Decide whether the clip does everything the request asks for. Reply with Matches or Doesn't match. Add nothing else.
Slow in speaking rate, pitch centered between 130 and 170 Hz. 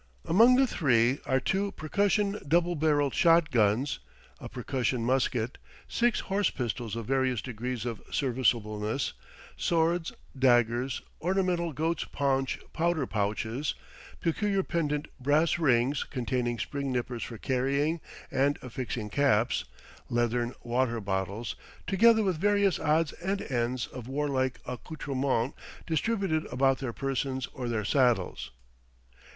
Matches